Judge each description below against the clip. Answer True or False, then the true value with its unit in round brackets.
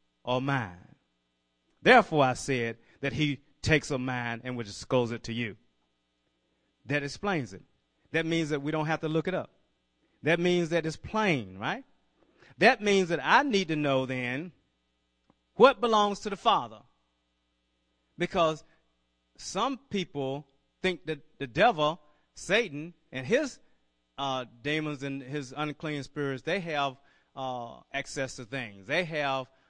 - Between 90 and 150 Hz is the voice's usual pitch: True (140 Hz)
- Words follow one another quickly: False (145 wpm)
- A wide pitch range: True (5.9 semitones)